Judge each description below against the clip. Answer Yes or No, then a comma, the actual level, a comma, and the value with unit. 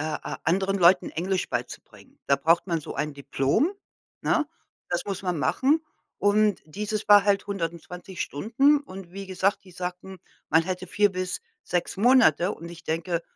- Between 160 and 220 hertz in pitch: Yes, medium, 185 Hz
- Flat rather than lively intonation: No, average, 3.2 semitones